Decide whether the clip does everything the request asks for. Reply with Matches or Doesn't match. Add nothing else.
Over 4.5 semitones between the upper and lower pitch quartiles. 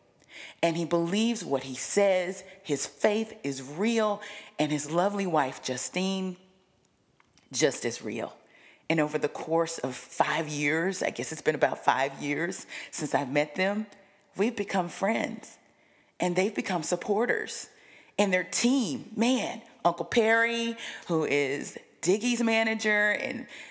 Matches